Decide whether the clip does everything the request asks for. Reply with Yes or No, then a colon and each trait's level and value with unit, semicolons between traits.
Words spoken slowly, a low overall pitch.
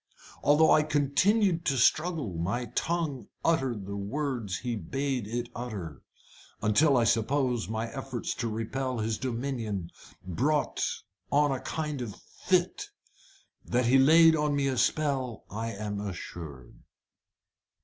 Yes: slow, 130 wpm; low, 125 Hz